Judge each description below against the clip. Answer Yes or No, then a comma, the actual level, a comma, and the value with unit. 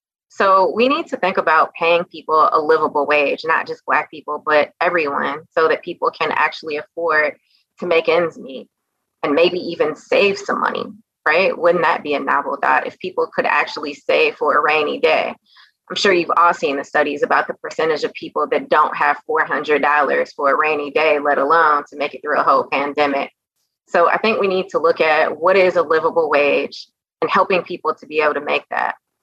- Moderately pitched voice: Yes, medium, 170 Hz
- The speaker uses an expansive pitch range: Yes, wide, 7.5 semitones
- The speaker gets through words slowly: No, fast, 205 wpm